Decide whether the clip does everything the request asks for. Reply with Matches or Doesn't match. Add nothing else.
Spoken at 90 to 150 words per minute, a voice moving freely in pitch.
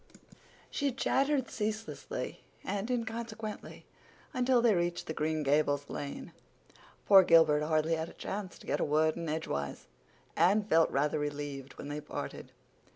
Matches